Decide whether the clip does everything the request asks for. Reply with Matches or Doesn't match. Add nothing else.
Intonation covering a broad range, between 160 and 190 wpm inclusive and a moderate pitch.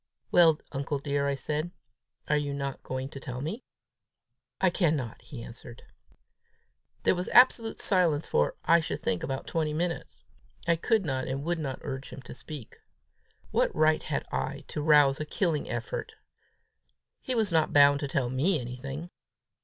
Doesn't match